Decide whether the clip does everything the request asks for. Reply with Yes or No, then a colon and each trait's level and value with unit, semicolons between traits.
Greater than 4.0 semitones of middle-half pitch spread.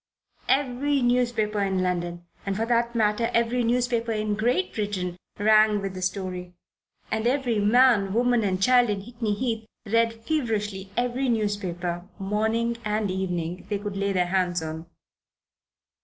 No: average, 3.6 semitones